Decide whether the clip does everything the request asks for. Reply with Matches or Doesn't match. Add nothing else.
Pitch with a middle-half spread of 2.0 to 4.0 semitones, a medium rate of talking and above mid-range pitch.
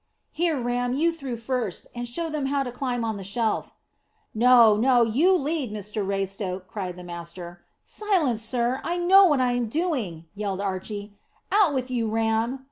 Doesn't match